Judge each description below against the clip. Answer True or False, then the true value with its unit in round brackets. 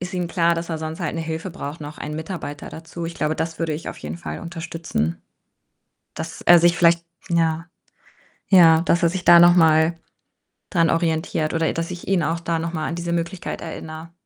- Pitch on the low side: False (165 Hz)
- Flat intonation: True (1.2 semitones)